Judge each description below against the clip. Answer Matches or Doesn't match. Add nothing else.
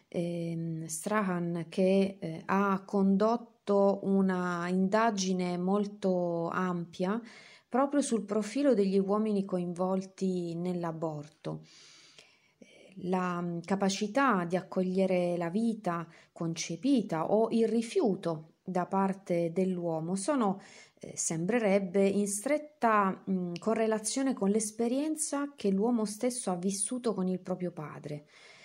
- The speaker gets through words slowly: Matches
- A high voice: Matches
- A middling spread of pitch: Matches